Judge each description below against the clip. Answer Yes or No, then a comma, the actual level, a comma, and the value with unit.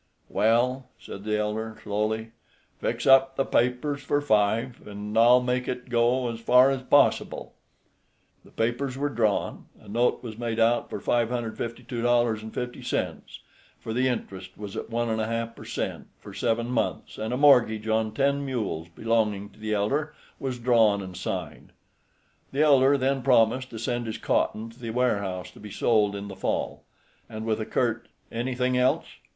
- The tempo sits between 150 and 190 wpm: Yes, average, 170 wpm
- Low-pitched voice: Yes, low, 115 Hz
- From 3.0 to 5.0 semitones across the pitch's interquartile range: No, narrow, 2.6 semitones